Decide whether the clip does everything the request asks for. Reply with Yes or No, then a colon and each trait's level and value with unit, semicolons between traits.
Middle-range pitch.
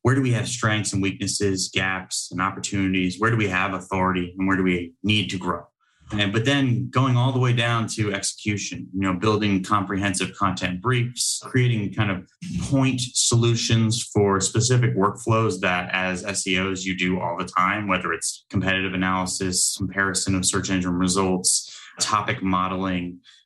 No: very low, 95 Hz